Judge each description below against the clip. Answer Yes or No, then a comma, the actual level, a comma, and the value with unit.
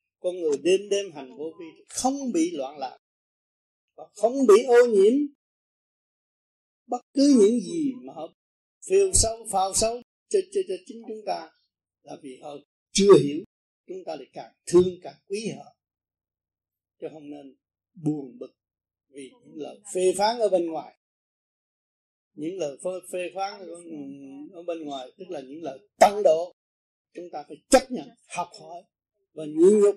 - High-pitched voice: Yes, high, 200 Hz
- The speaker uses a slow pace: Yes, slow, 160 wpm